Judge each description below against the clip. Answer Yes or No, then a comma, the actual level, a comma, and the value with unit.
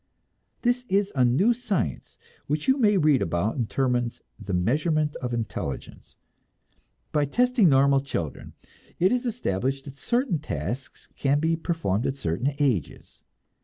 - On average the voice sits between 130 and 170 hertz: Yes, medium, 140 Hz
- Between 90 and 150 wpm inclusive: Yes, average, 140 wpm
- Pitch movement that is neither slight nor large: No, wide, 7.5 semitones